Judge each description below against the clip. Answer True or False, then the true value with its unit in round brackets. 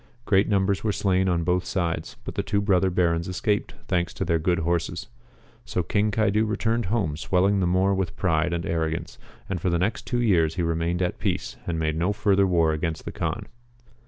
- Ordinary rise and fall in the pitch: True (3.0 semitones)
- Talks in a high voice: False (90 Hz)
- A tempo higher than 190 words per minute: True (205 wpm)